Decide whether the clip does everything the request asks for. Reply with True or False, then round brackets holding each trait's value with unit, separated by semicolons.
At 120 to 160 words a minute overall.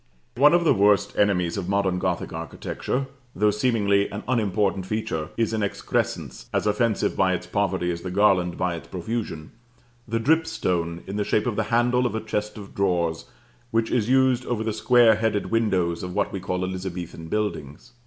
False (185 wpm)